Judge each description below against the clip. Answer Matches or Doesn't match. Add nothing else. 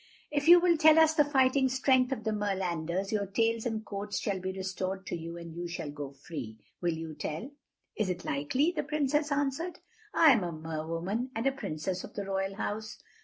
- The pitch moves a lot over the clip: Matches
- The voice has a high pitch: Matches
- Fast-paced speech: Matches